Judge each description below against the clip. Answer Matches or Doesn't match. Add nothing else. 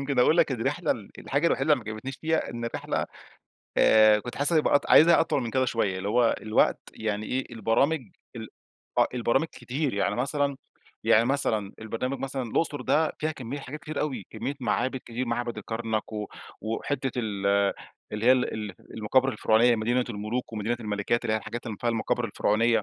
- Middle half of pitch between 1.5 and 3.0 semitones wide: Doesn't match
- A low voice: Matches